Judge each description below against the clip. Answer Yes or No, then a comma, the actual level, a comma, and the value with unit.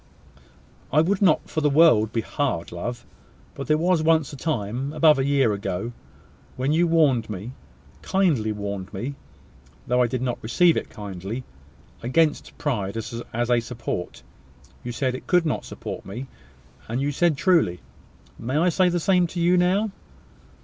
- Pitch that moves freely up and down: Yes, wide, 6.4 semitones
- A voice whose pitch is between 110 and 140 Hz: Yes, low, 135 Hz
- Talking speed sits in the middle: Yes, average, 165 wpm